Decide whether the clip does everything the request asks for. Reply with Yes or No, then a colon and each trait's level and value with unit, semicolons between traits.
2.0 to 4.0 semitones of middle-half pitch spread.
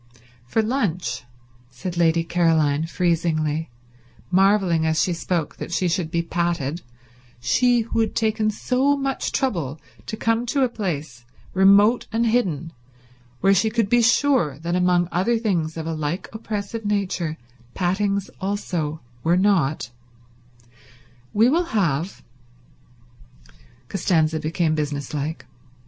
No: average, 5.2 semitones